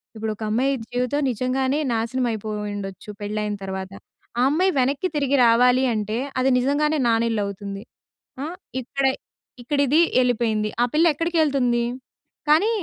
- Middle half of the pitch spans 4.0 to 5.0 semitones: Yes, average, 4.5 semitones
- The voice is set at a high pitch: Yes, high, 245 Hz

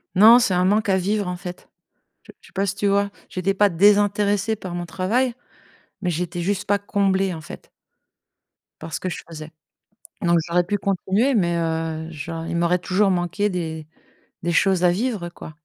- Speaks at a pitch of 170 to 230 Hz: Yes, medium, 185 Hz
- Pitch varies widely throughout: No, average, 2.8 semitones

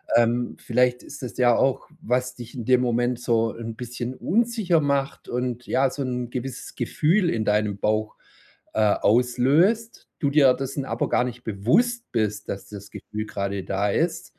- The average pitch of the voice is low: Yes, low, 125 Hz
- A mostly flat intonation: No, average, 3.3 semitones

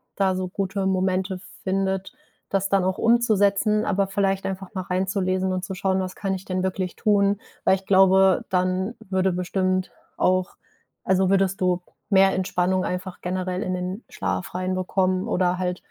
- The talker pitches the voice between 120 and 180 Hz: No, high, 190 Hz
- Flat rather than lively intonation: Yes, narrow, 0.9 semitones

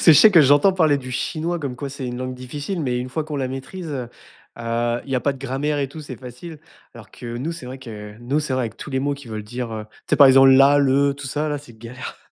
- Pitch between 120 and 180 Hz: Yes, low, 135 Hz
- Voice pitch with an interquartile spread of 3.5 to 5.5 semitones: No, average, 2.8 semitones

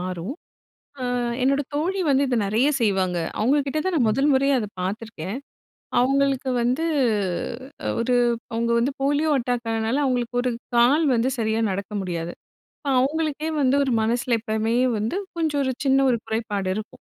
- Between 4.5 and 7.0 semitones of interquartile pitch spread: No, average, 4.0 semitones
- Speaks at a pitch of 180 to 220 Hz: No, high, 245 Hz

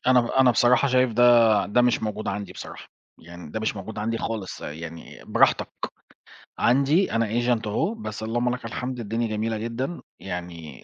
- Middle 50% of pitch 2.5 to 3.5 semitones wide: Yes, average, 3.2 semitones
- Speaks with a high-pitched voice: No, low, 115 Hz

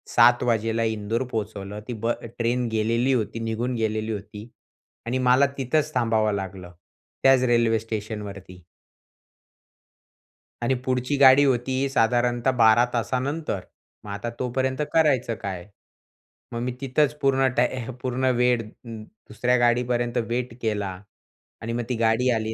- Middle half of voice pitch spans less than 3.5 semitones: Yes, narrow, 2.5 semitones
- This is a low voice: Yes, low, 120 Hz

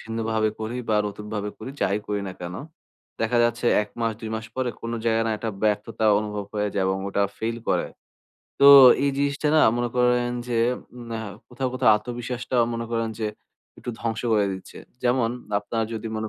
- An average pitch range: No, narrow, 2.3 semitones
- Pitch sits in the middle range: No, low, 115 Hz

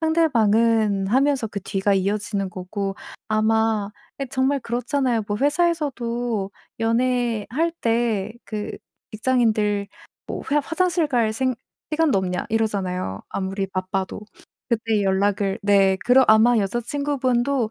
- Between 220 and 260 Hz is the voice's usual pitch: Yes, high, 225 Hz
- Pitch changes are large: No, average, 4.3 semitones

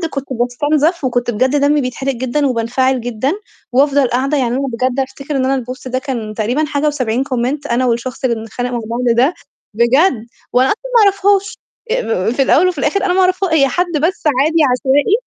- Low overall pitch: No, very high, 265 Hz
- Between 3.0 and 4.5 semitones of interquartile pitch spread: Yes, average, 3.6 semitones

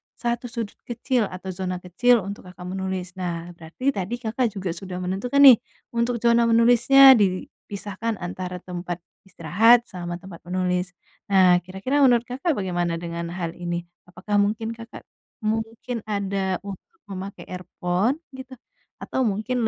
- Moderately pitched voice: No, high, 195 Hz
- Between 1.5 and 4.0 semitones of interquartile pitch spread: No, average, 4.5 semitones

